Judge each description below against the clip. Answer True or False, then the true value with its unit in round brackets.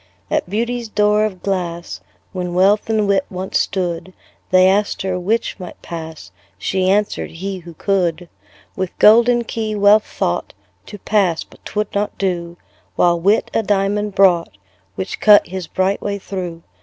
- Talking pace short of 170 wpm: True (155 wpm)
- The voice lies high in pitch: True (195 Hz)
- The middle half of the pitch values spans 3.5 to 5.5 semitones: False (2.7 semitones)